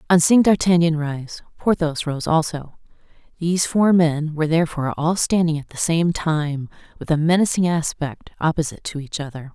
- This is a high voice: No, medium, 160 Hz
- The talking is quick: No, average, 165 wpm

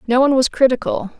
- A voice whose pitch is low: No, very high, 255 Hz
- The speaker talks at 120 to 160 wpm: No, average, 200 wpm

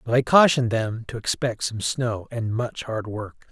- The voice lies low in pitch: Yes, low, 115 Hz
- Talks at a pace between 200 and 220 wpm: Yes, fast, 205 wpm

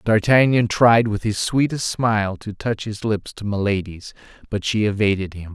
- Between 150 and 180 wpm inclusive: Yes, average, 175 wpm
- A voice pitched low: Yes, low, 105 Hz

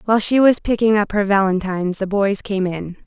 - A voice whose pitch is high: Yes, high, 200 Hz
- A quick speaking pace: Yes, fast, 215 wpm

